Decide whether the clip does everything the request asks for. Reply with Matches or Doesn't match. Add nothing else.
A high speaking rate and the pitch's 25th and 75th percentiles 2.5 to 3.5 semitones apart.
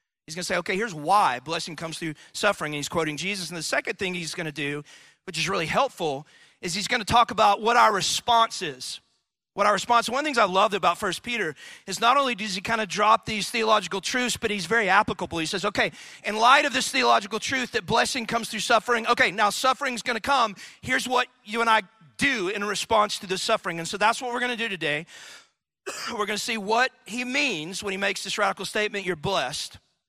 Doesn't match